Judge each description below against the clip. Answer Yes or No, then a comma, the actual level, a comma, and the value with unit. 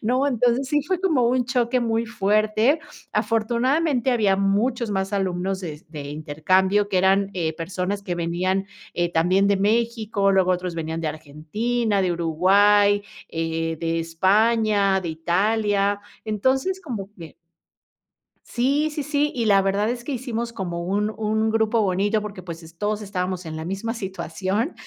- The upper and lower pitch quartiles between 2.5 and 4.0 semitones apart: No, average, 4.5 semitones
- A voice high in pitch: Yes, high, 200 Hz